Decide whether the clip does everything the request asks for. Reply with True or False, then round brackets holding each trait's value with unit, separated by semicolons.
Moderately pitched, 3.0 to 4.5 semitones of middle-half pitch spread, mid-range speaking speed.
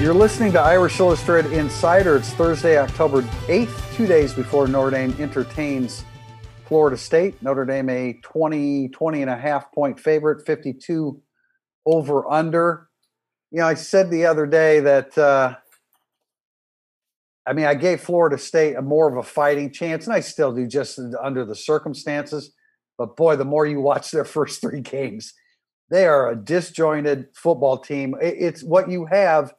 True (145 Hz; 3.3 semitones; 160 wpm)